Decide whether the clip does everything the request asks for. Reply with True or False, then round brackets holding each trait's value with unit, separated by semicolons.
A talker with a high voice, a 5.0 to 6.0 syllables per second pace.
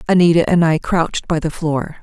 False (165 Hz; 5.5 syllables/s)